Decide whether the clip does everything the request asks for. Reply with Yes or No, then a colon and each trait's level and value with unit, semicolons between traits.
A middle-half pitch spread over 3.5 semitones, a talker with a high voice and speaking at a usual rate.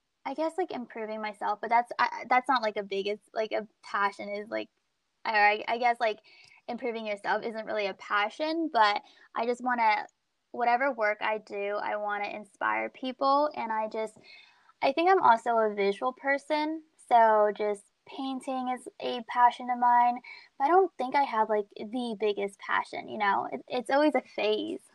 Yes: average, 4.6 semitones; high, 235 Hz; average, 185 wpm